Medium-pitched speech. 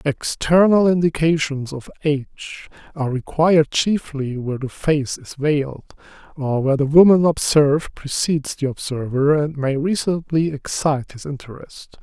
Yes: medium, 150 Hz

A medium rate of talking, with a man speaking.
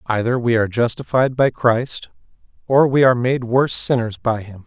Yes: average, 180 wpm; male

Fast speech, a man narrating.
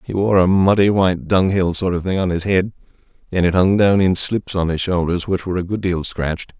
Yes: fast, 245 wpm; male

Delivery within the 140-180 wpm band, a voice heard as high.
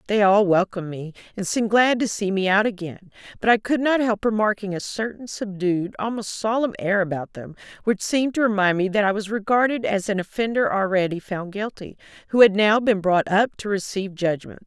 No: fast, 205 wpm; high, 205 Hz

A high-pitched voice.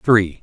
No: low, 100 Hz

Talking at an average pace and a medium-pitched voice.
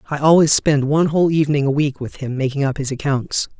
No: fast, 235 wpm; medium, 145 Hz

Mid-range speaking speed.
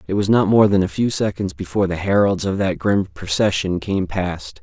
No: fast, 220 wpm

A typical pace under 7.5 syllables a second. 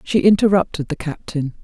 Yes: 5.3 syllables/s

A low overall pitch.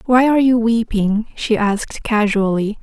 No: high, 220 Hz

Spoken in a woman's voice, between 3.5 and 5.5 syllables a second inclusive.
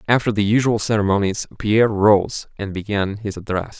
No: male; 5.3 syllables/s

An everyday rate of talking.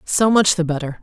No: fast, 235 wpm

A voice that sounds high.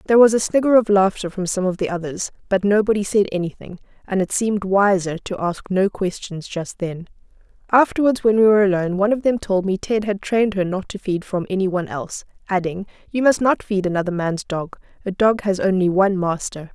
Yes: high, 195 Hz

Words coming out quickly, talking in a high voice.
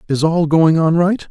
No: fast, 230 wpm; medium, 165 Hz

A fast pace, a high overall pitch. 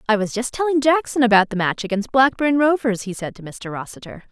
Yes: fast, 225 wpm; high, 235 Hz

